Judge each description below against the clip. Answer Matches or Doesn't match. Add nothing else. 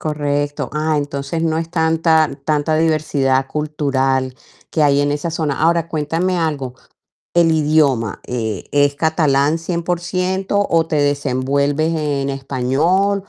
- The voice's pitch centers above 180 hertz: Doesn't match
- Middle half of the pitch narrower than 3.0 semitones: Matches